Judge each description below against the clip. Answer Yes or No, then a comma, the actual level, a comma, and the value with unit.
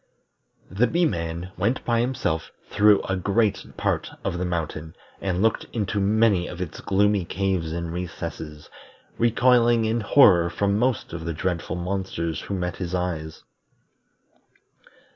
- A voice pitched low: Yes, very low, 95 Hz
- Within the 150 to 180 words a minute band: No, average, 140 wpm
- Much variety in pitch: No, average, 4.3 semitones